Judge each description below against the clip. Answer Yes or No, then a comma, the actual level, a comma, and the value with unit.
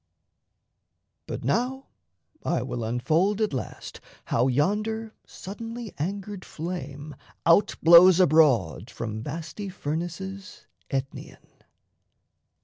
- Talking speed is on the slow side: Yes, slow, 90 wpm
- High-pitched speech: No, medium, 170 Hz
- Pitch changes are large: Yes, wide, 6.3 semitones